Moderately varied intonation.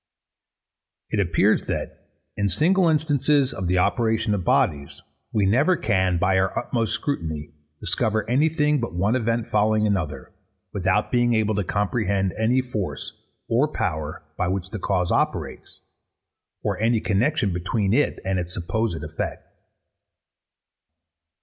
Yes: average, 4.7 semitones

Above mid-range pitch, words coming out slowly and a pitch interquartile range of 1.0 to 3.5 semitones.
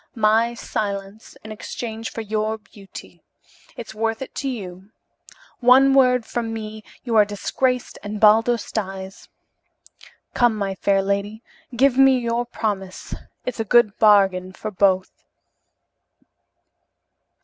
Yes: high, 220 Hz; slow, 125 wpm; average, 2.9 semitones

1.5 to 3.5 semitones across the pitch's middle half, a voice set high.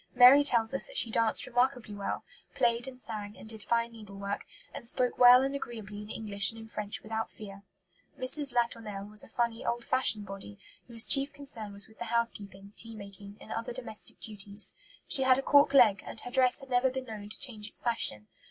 Yes: average, 3.2 semitones; high, 230 Hz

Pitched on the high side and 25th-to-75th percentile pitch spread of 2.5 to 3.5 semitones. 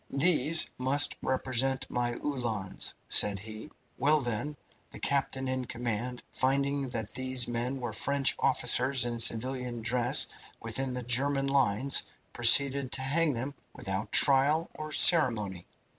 No: low, 130 Hz; average, 2.9 semitones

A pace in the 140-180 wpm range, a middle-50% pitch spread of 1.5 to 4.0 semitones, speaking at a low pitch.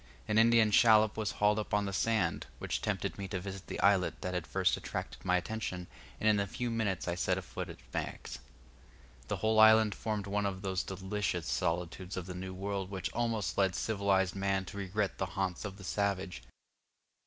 No: average, 200 wpm; narrow, 2.4 semitones; low, 100 Hz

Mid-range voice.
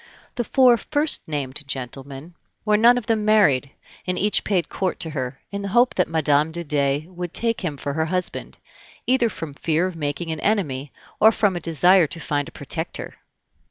Yes: medium, 170 Hz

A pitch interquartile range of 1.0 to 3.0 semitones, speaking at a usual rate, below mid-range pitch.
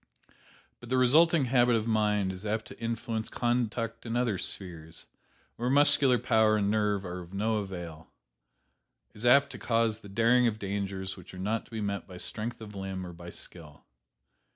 No: average, 3.6 semitones; average, 180 wpm; low, 110 Hz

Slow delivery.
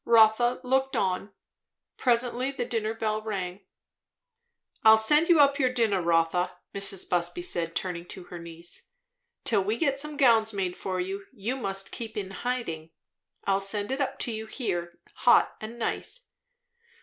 No: average, 160 wpm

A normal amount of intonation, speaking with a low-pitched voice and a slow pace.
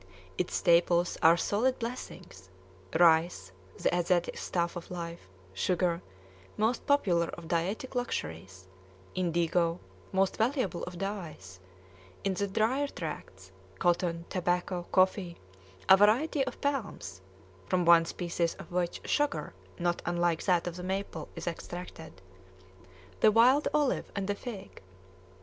No: average, 3.1 semitones; medium, 175 Hz; slow, 125 wpm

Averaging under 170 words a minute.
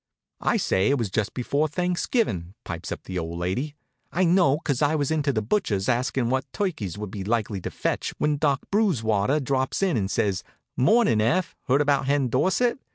No: average, 190 wpm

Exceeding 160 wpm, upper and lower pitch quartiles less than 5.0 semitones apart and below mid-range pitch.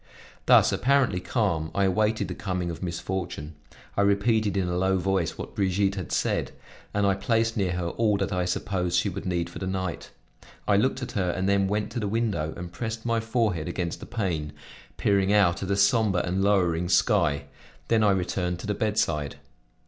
Yes: average, 195 wpm; average, 3.0 semitones; very low, 95 Hz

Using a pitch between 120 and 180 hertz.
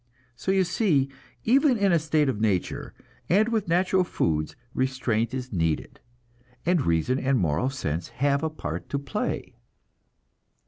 Yes: low, 135 Hz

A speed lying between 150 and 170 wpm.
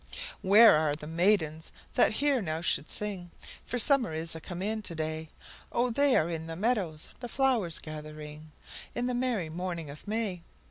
No: average, 180 wpm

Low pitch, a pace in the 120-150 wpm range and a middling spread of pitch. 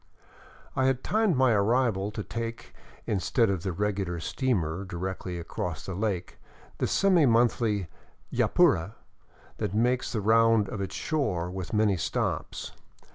Yes: low, 105 Hz; average, 145 wpm; average, 4.1 semitones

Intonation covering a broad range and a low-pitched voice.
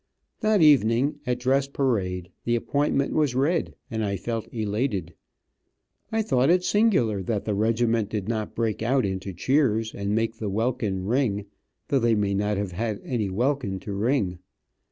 No: average, 4.8 semitones; low, 115 Hz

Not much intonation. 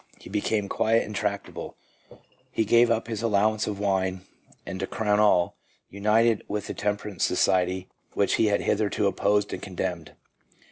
Yes: narrow, 2.0 semitones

